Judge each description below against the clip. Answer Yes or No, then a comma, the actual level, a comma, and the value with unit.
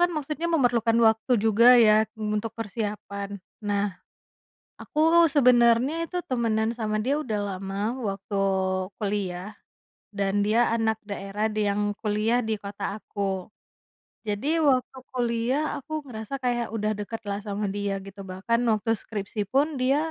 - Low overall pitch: No, high, 220 Hz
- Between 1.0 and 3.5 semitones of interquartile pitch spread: Yes, average, 2.9 semitones